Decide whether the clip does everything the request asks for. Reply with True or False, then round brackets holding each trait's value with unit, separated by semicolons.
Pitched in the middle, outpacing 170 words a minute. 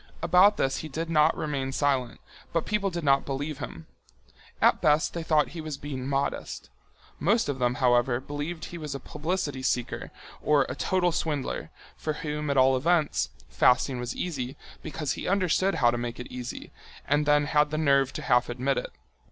True (145 Hz; 185 wpm)